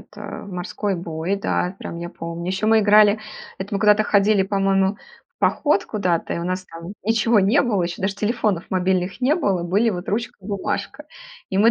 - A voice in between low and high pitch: No, high, 195 Hz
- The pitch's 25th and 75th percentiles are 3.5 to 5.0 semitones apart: No, average, 2.8 semitones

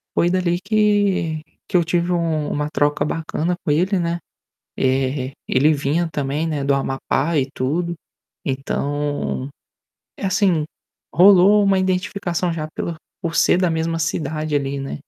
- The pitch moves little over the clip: No, average, 3.5 semitones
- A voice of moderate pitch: Yes, medium, 160 Hz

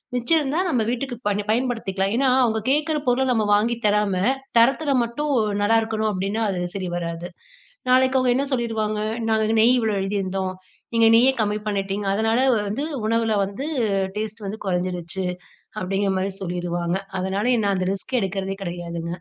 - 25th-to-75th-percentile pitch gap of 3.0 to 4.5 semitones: Yes, average, 3.7 semitones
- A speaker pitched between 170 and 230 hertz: Yes, high, 210 Hz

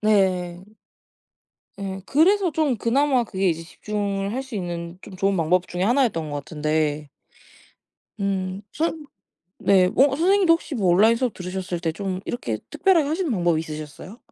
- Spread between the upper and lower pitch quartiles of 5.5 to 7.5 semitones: Yes, wide, 6.8 semitones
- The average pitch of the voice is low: No, high, 195 Hz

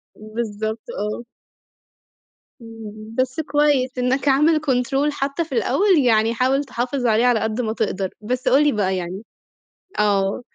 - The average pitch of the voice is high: Yes, high, 245 Hz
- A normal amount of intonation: Yes, average, 4.0 semitones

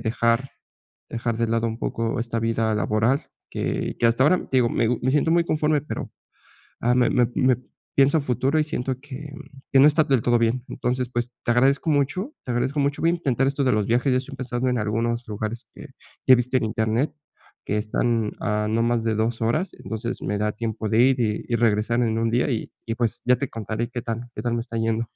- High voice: No, low, 120 Hz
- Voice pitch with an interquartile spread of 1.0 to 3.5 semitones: Yes, average, 2.7 semitones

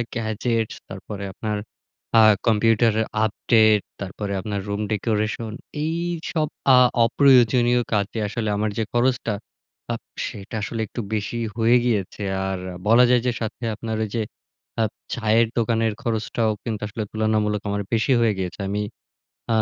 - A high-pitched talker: No, low, 110 Hz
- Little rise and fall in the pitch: Yes, narrow, 1.9 semitones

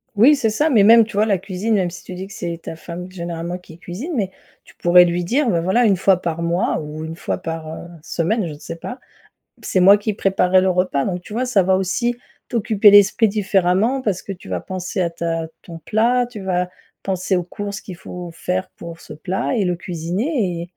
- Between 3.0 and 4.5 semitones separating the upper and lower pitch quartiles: Yes, average, 3.4 semitones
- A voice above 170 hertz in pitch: Yes, medium, 185 Hz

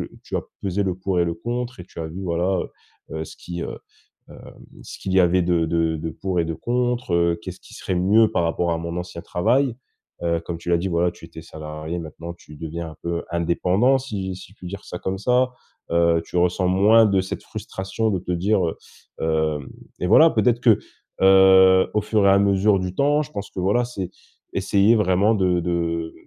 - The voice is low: Yes, very low, 90 Hz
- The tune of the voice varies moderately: Yes, average, 3.1 semitones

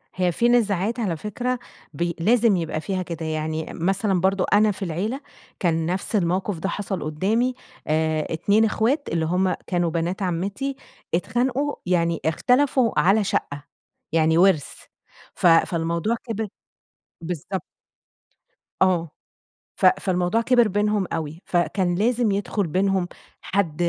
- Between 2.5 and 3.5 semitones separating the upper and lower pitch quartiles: No, average, 4.3 semitones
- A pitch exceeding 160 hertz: Yes, medium, 185 Hz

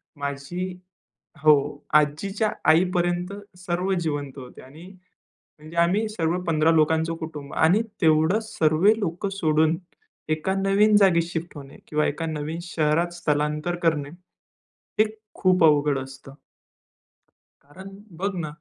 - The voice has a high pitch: No, medium, 165 Hz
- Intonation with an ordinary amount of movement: Yes, average, 3.0 semitones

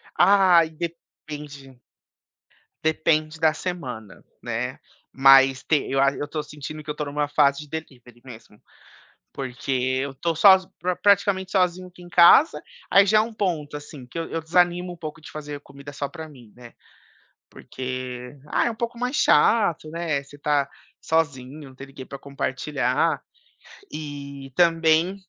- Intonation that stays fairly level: No, average, 3.8 semitones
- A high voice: No, medium, 150 Hz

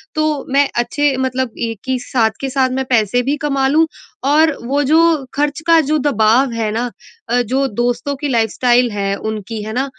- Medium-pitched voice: No, very high, 255 Hz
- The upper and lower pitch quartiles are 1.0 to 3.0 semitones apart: No, average, 3.6 semitones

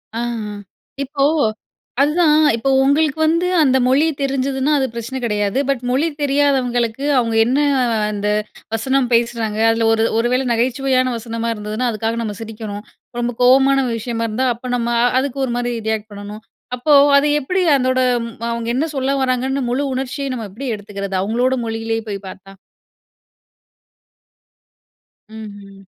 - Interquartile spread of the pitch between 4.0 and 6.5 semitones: No, average, 3.2 semitones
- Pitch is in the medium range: No, high, 245 Hz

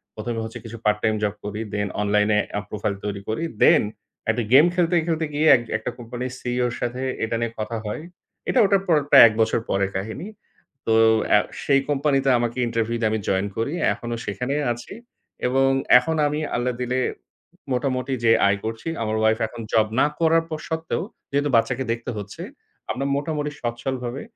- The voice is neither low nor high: No, low, 120 Hz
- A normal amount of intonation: Yes, average, 4.1 semitones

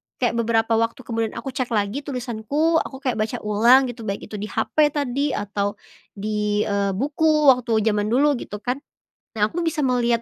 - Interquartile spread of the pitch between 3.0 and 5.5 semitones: Yes, average, 4.4 semitones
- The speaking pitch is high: Yes, high, 235 Hz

